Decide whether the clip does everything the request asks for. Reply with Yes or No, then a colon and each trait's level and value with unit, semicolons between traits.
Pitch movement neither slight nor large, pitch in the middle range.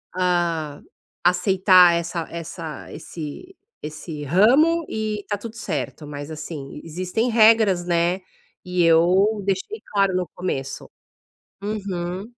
Yes: average, 3.8 semitones; medium, 180 Hz